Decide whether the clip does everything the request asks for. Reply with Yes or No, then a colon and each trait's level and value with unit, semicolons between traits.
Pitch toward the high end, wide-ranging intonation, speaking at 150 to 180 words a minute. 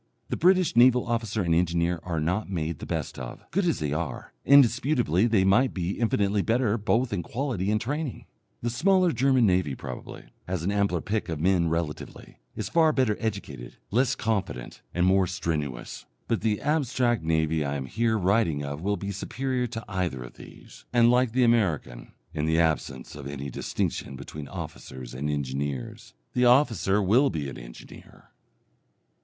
No: low, 100 Hz; wide, 7.1 semitones; average, 170 wpm